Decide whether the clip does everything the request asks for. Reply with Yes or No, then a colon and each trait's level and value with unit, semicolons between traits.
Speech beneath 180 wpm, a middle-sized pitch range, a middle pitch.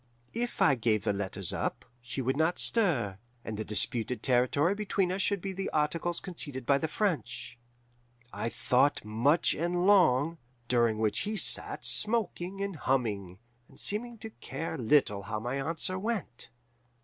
No: average, 160 wpm; wide, 7.8 semitones; medium, 145 Hz